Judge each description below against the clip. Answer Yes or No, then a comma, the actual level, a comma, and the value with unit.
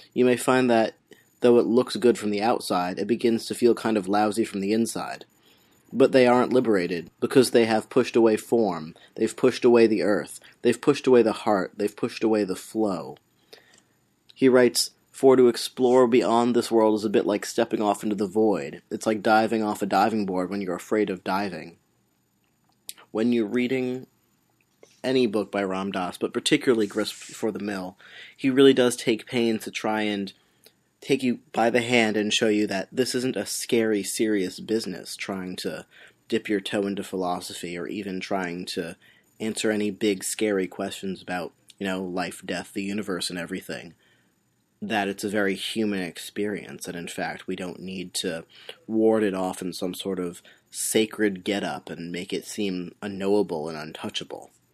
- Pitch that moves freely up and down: No, average, 3.3 semitones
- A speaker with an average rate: Yes, average, 180 wpm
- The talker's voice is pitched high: No, low, 105 Hz